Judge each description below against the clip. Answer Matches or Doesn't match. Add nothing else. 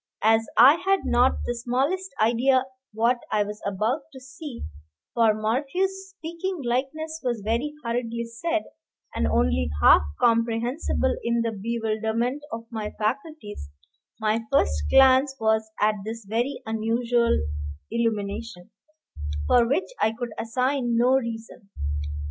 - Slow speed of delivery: Matches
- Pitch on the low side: Doesn't match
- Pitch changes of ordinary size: Matches